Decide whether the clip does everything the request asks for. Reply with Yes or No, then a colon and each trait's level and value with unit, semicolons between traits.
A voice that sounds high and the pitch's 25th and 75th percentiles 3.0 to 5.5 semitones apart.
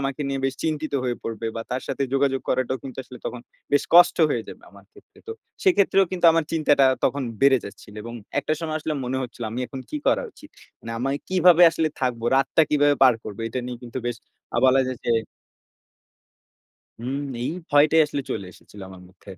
No: low, 135 Hz; average, 4.1 semitones